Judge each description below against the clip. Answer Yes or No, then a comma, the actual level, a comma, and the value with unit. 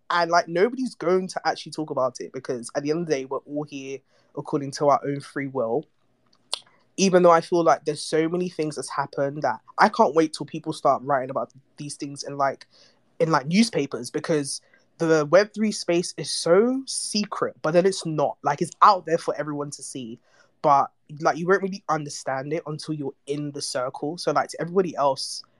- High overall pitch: No, medium, 155 Hz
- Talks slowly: No, fast, 205 wpm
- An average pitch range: Yes, average, 3.5 semitones